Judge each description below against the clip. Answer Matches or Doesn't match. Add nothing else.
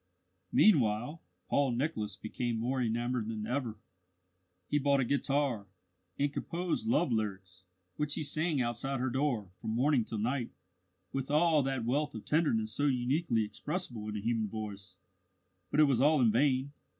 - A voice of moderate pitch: Doesn't match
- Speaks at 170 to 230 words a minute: Doesn't match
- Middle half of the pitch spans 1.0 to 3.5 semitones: Doesn't match